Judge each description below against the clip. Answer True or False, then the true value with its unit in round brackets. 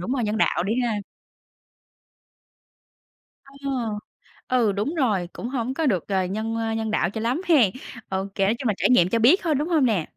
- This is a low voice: False (225 Hz)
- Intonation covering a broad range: False (4.6 semitones)